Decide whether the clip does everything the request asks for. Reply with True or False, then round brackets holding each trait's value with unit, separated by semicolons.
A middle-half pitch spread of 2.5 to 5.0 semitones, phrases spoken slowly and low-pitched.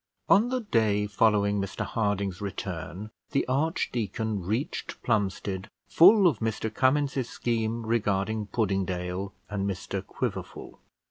True (3.4 semitones; 115 wpm; 105 Hz)